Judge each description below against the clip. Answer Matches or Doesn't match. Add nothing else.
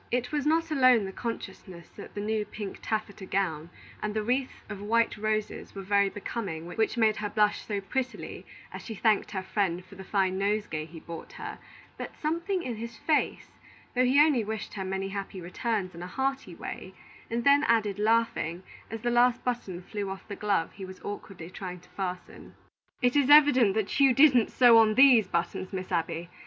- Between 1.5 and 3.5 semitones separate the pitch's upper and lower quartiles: Doesn't match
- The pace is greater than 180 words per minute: Matches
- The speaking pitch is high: Matches